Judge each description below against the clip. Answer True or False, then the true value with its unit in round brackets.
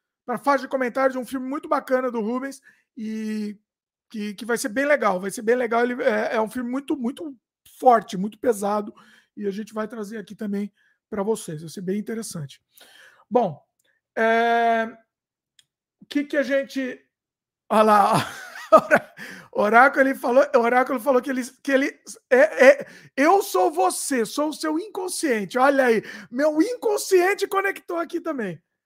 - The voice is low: False (250 Hz)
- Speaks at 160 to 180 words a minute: True (165 wpm)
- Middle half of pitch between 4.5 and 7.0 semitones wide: True (4.8 semitones)